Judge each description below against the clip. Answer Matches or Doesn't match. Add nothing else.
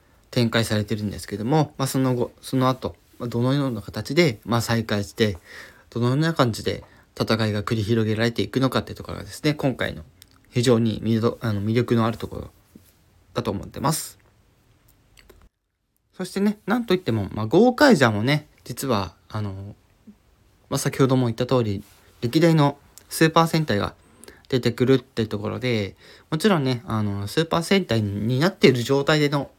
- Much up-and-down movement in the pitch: Doesn't match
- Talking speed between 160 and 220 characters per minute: Doesn't match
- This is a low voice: Matches